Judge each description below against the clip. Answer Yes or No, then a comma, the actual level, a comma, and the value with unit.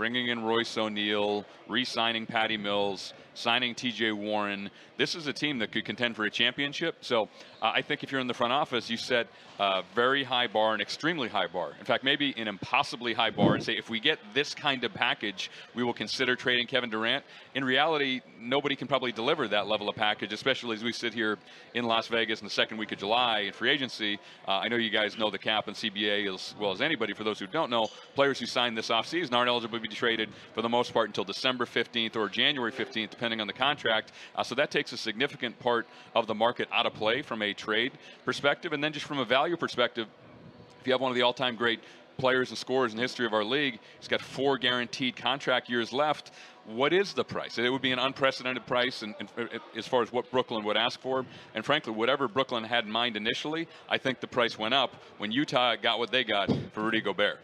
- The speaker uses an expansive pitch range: No, average, 2.8 semitones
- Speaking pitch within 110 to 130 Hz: Yes, low, 120 Hz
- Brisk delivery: Yes, fast, 235 wpm